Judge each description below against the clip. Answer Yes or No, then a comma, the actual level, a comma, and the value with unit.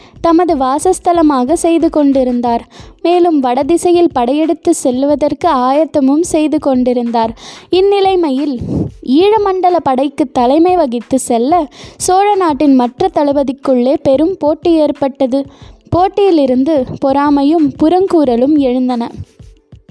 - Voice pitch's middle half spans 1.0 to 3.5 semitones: No, average, 4.2 semitones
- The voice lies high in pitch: Yes, very high, 295 Hz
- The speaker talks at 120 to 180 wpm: No, average, 85 wpm